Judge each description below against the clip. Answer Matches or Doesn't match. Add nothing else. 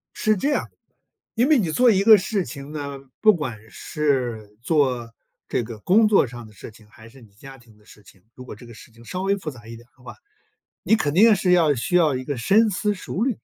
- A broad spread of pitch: Matches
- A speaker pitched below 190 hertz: Matches